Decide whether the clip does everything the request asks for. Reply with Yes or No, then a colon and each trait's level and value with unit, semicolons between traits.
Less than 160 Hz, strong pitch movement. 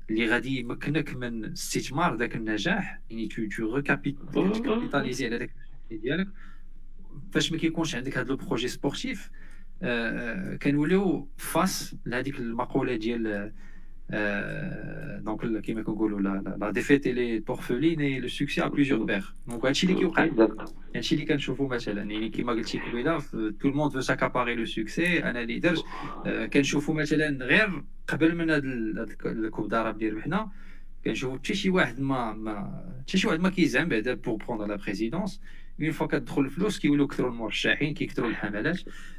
Yes: medium, 140 Hz; wide, 6.0 semitones